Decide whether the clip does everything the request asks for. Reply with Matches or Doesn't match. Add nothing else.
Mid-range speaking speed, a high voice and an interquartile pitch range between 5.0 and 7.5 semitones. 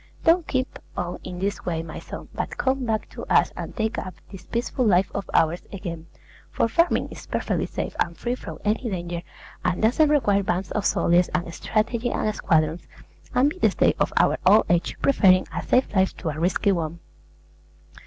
Matches